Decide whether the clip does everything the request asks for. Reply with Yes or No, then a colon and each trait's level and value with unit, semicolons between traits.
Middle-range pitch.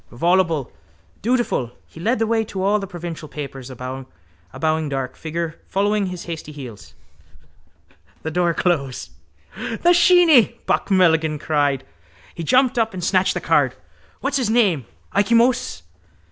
Yes: medium, 170 Hz